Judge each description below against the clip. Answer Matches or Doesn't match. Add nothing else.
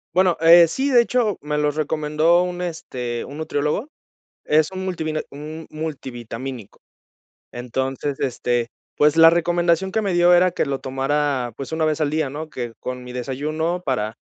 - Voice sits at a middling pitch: Matches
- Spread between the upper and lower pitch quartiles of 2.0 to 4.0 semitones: Doesn't match